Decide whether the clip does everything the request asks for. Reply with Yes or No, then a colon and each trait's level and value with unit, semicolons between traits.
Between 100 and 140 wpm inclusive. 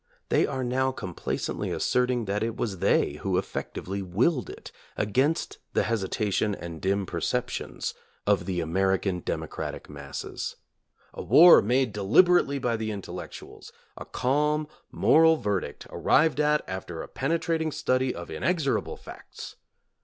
Yes: slow, 135 wpm